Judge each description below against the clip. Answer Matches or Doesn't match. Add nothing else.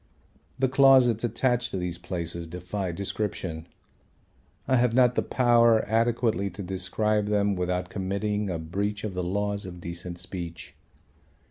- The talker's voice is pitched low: Matches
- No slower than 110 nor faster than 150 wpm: Matches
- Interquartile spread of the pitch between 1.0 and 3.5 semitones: Doesn't match